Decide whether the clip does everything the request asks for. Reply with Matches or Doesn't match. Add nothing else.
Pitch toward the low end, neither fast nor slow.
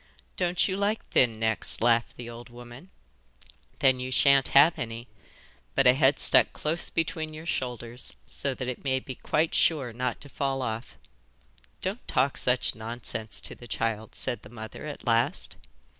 Matches